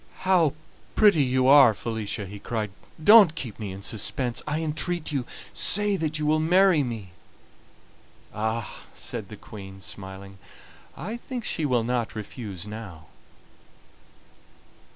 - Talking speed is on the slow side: Yes, slow, 130 wpm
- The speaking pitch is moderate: No, low, 125 Hz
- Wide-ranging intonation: Yes, wide, 6.9 semitones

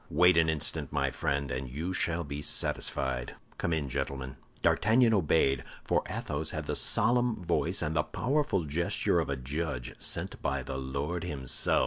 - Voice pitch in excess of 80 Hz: No, very low, 75 Hz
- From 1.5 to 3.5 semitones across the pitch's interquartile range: No, average, 4.5 semitones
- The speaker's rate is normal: Yes, average, 165 wpm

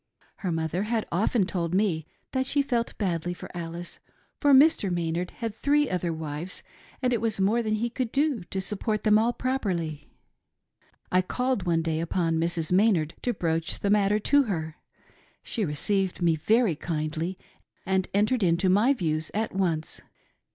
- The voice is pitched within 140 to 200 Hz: Yes, high, 190 Hz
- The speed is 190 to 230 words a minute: No, average, 170 wpm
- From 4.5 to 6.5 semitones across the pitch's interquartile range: Yes, average, 5.2 semitones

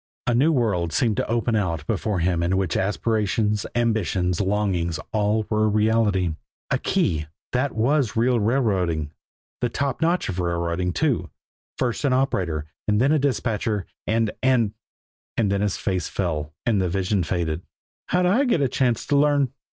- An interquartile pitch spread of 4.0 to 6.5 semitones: Yes, average, 5.2 semitones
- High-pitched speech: No, low, 105 Hz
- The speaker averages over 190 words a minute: No, average, 165 wpm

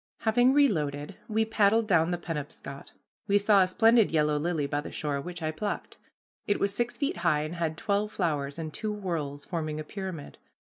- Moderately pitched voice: Yes, medium, 170 Hz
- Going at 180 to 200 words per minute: Yes, average, 190 wpm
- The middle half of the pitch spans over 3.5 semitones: Yes, wide, 5.5 semitones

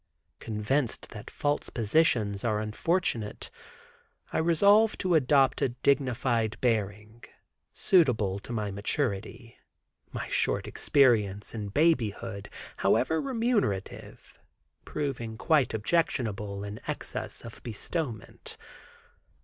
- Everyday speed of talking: No, slow, 95 wpm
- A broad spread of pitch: Yes, wide, 5.9 semitones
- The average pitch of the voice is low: Yes, low, 120 Hz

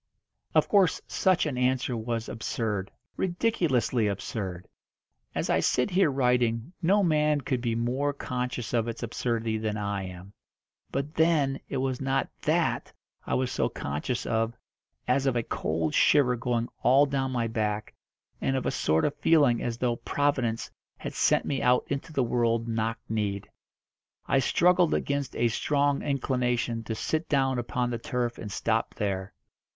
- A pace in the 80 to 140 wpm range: No, average, 160 wpm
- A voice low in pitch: Yes, low, 125 Hz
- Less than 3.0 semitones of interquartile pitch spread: No, average, 3.5 semitones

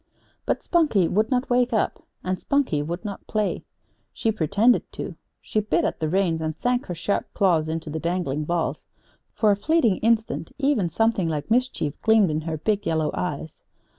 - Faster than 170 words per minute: Yes, average, 180 wpm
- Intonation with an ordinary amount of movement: No, wide, 5.8 semitones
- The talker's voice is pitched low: No, high, 195 Hz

